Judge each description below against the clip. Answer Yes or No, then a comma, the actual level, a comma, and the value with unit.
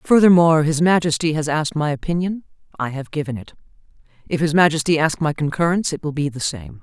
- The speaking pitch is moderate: Yes, medium, 155 Hz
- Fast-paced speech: No, average, 195 wpm